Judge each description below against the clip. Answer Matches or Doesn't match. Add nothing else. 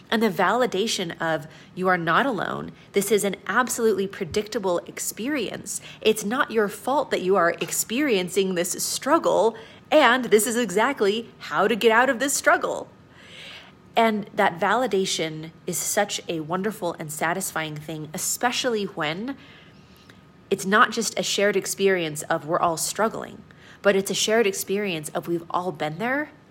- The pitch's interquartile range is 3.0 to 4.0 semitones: Doesn't match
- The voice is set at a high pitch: Matches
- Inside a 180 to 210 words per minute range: Doesn't match